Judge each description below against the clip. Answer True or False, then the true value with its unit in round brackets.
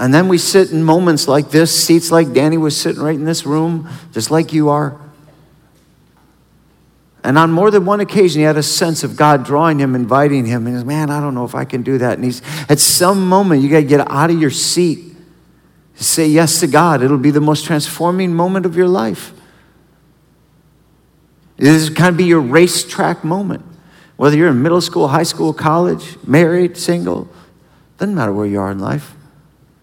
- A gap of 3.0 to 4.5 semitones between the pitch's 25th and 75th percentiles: False (2.6 semitones)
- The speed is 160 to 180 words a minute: False (195 wpm)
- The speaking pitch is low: False (155 Hz)